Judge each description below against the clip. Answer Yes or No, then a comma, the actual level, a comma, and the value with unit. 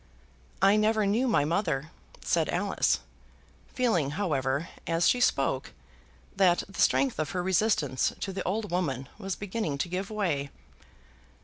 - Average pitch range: No, wide, 6.0 semitones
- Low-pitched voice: No, medium, 185 Hz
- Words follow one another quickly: No, average, 140 wpm